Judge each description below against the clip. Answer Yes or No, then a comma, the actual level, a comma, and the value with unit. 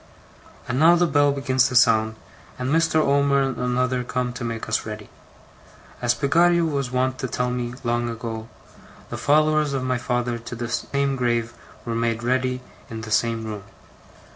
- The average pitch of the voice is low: Yes, low, 125 Hz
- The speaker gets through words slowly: No, average, 175 wpm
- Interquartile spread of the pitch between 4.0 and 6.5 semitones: No, average, 2.8 semitones